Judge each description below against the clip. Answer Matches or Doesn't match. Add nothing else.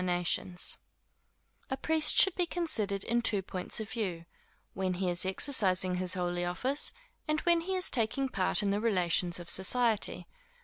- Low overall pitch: Doesn't match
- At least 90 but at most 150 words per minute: Doesn't match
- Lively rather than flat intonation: Matches